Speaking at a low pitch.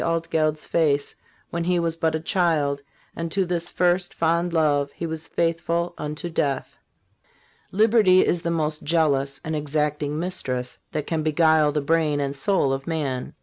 No: medium, 160 Hz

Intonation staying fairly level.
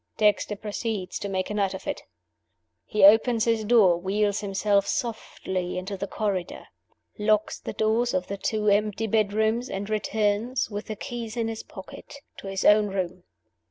Yes: narrow, 2.0 semitones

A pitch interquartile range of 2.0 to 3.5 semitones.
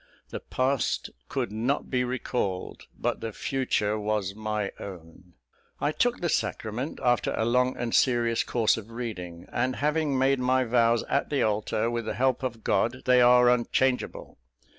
Yes: average, 3.1 semitones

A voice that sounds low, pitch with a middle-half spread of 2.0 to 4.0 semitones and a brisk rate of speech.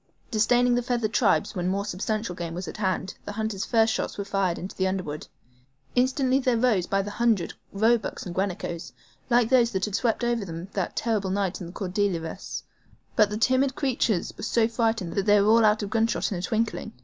No: high, 210 Hz; average, 3.6 semitones; fast, 210 wpm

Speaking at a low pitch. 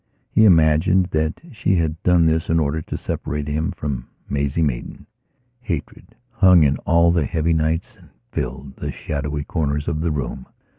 Yes: very low, 80 Hz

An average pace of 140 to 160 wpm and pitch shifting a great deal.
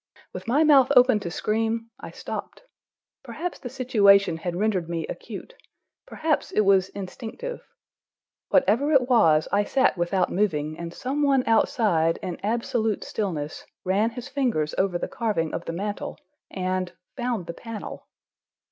Yes: average, 145 wpm; wide, 5.8 semitones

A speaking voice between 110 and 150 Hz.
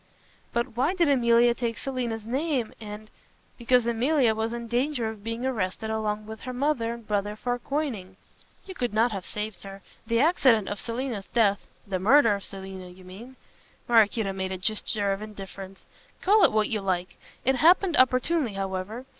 No: high, 225 Hz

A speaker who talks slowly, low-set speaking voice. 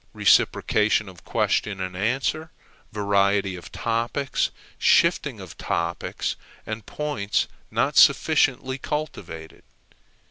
Yes: slow, 95 wpm; low, 105 Hz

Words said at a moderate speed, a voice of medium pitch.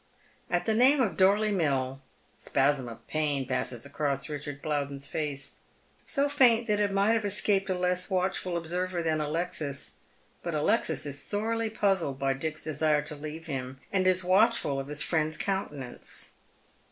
Yes: average, 165 wpm; medium, 160 Hz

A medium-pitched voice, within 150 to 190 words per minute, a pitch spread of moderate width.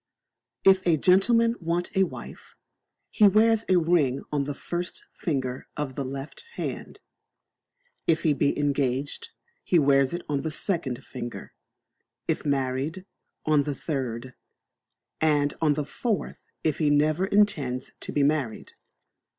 No: medium, 150 Hz; average, 140 wpm; average, 4.4 semitones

